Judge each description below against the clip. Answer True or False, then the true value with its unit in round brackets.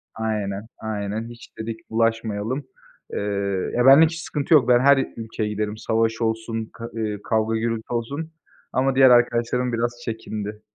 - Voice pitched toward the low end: True (115 Hz)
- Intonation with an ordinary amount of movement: False (1.9 semitones)